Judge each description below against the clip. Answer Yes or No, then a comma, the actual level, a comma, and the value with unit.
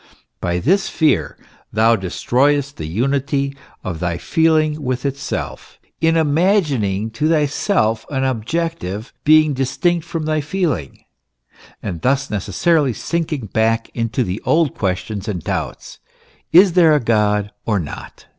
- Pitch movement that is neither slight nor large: No, wide, 6.5 semitones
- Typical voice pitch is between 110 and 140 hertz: Yes, low, 135 Hz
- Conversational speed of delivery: No, slow, 130 wpm